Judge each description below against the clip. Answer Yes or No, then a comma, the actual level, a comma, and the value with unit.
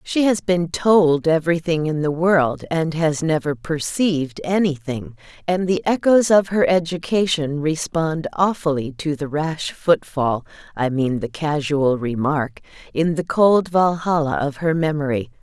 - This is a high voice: No, medium, 160 Hz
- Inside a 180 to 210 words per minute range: No, slow, 135 wpm